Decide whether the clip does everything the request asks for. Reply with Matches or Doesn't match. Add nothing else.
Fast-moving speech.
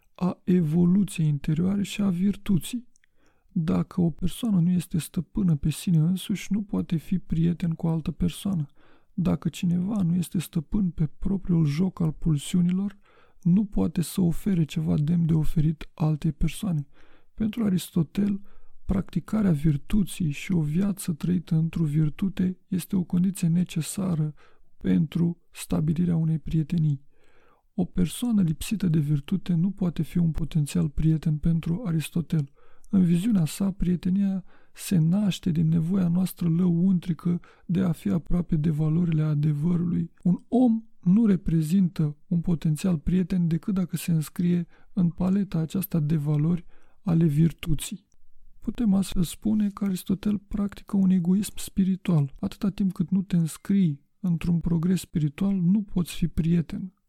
Doesn't match